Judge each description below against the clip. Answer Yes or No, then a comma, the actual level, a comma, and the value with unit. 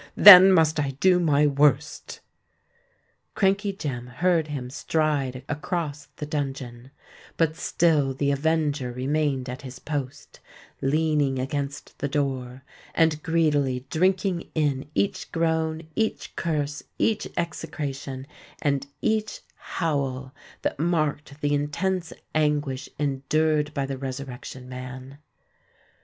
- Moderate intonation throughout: Yes, average, 3.1 semitones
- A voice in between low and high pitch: Yes, medium, 145 Hz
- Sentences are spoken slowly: Yes, slow, 105 wpm